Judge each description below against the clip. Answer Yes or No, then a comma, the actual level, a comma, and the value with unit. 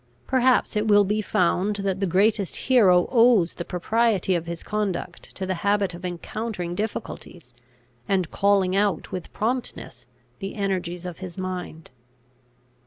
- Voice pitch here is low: No, high, 195 Hz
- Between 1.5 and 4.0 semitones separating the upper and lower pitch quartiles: Yes, average, 2.9 semitones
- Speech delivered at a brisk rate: No, average, 145 wpm